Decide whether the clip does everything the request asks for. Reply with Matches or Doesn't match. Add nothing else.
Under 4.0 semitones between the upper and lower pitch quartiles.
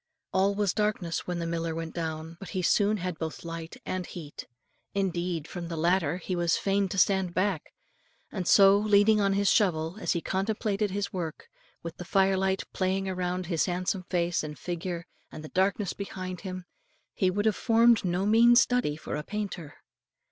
Matches